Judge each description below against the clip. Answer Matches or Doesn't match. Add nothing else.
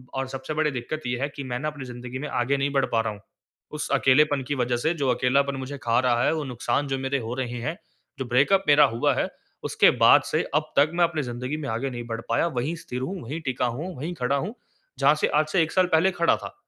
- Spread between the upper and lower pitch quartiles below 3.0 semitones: Doesn't match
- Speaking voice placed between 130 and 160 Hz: Matches